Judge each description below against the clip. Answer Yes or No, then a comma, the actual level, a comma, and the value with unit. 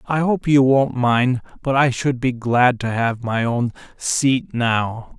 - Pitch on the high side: No, low, 125 Hz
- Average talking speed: Yes, average, 185 wpm